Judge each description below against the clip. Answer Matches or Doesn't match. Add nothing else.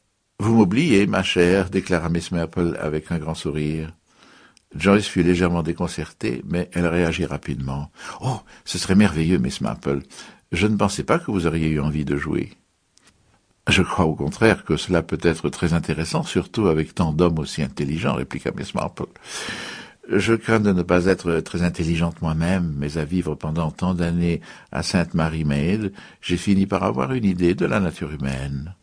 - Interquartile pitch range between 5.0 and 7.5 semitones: Doesn't match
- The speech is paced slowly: Doesn't match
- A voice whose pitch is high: Doesn't match